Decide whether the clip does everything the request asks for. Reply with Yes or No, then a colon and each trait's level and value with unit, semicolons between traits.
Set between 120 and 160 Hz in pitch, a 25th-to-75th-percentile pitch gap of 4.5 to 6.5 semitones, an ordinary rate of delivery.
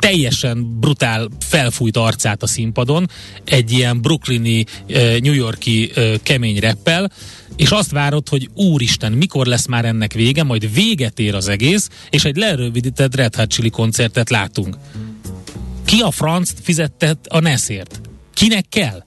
Yes: low, 125 Hz; average, 5.1 semitones; average, 140 wpm